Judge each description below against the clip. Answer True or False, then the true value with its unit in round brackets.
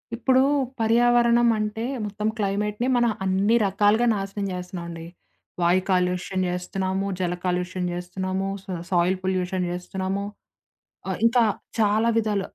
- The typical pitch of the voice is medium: False (195 Hz)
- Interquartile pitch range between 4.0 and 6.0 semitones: False (2.9 semitones)